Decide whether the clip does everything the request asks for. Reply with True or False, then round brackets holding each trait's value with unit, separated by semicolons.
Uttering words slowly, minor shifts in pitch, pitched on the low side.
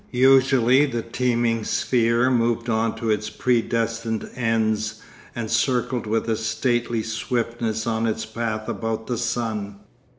True (130 wpm; 1.4 semitones; 115 Hz)